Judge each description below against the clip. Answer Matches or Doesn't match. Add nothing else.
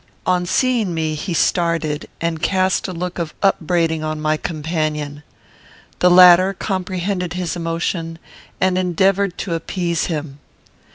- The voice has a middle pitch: Matches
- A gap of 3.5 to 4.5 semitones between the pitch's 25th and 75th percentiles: Doesn't match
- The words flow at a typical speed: Doesn't match